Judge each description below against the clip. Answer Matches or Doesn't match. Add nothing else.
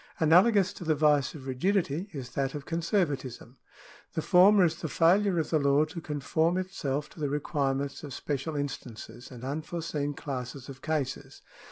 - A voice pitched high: Doesn't match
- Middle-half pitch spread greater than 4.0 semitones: Doesn't match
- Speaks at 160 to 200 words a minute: Matches